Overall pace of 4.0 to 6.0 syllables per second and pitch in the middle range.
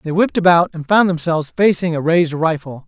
No: 6.3 syllables/s; medium, 165 Hz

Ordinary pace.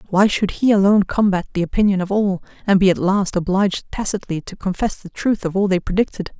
No: fast, 215 wpm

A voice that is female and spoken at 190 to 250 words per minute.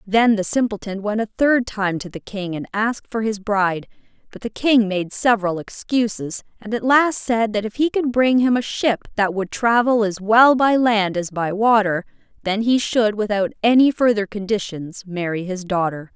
Yes: female; average, 195 wpm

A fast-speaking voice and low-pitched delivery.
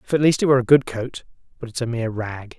Yes: fast, 300 wpm; low, 125 Hz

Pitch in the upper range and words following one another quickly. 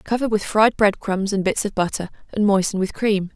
Yes: high, 200 Hz; fast, 235 wpm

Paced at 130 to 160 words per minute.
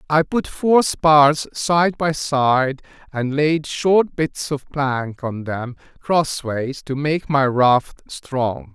Yes: average, 150 wpm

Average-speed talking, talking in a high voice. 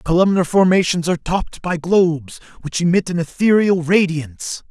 No: average, 155 wpm; medium, 175 Hz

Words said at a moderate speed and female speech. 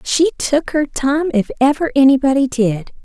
Yes: average, 160 wpm; female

